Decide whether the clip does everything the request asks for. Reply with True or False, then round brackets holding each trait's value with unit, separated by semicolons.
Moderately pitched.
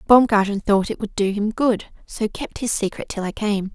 False (210 Hz)